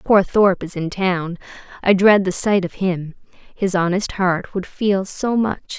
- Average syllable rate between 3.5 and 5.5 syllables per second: Yes, 4.0 syllables/s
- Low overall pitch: No, high, 190 Hz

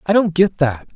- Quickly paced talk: Yes, fast, 250 wpm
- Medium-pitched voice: Yes, medium, 165 Hz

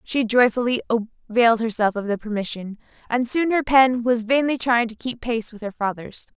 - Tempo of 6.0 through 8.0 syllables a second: No, 5.4 syllables/s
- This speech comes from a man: No, female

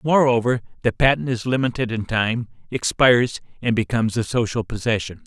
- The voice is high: No, low, 120 Hz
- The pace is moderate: Yes, average, 150 wpm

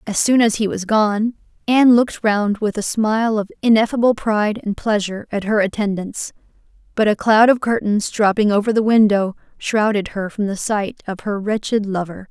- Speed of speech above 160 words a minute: Yes, average, 185 wpm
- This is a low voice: No, high, 210 Hz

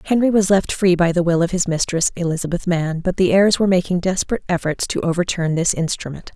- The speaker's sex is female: Yes, female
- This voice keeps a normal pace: No, fast, 215 wpm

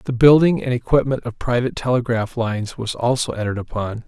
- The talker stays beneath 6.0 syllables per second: No, 6.1 syllables/s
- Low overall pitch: Yes, low, 120 Hz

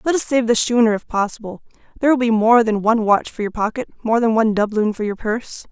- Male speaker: No, female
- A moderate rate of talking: No, fast, 250 wpm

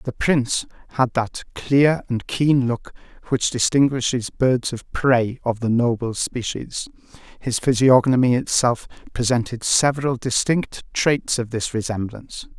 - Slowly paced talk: Yes, slow, 130 wpm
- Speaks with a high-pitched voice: No, low, 125 Hz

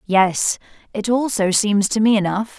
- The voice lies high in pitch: Yes, high, 205 Hz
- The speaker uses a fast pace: No, average, 165 wpm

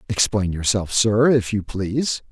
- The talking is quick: No, average, 155 wpm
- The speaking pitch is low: Yes, low, 105 Hz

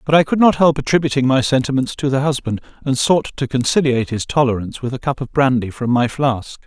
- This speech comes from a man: Yes, male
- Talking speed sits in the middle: No, fast, 225 wpm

